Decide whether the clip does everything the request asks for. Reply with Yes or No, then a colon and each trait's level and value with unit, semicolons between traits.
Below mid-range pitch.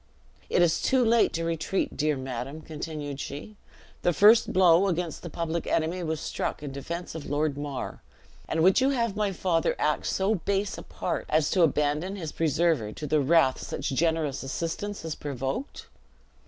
No: medium, 165 Hz